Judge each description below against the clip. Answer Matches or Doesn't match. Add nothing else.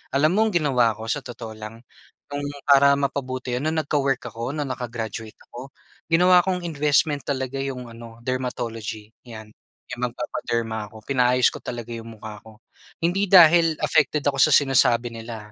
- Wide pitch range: Doesn't match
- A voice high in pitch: Doesn't match